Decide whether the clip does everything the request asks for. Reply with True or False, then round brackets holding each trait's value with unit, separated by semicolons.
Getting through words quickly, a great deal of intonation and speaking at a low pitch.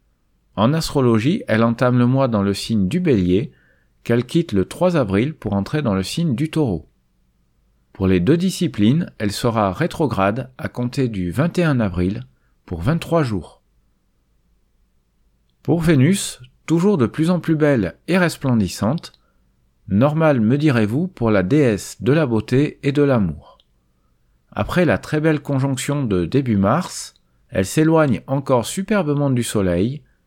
False (145 wpm; 7.9 semitones; 125 Hz)